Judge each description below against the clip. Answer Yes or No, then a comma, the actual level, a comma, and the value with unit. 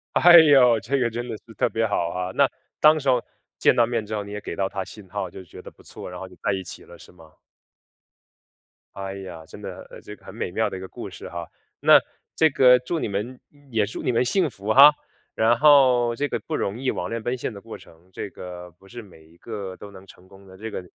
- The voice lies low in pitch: Yes, low, 105 Hz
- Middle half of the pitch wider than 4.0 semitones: Yes, average, 4.7 semitones